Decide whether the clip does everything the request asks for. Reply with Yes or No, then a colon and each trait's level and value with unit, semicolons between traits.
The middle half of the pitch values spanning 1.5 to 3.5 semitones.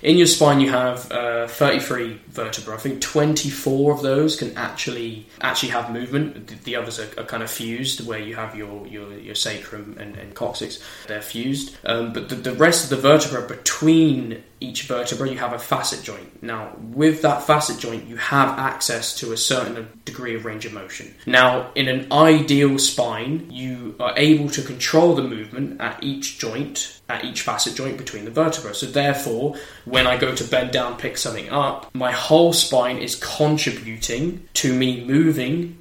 No: average, 3.9 semitones